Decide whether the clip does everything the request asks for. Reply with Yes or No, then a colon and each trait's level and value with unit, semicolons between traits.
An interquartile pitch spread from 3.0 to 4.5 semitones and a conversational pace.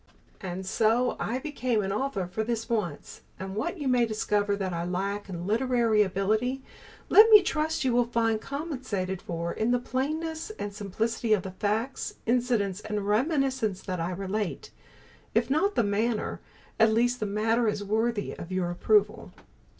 Yes: average, 4.0 semitones; average, 165 wpm